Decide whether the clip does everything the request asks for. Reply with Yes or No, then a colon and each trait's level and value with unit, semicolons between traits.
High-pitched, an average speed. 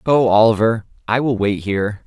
No: low, 110 Hz; average, 175 wpm